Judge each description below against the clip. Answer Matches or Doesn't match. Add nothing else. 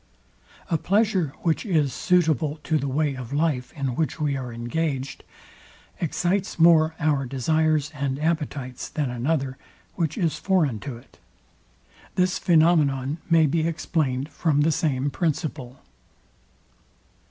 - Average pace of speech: Doesn't match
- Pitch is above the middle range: Doesn't match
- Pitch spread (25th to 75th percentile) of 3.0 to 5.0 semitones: Matches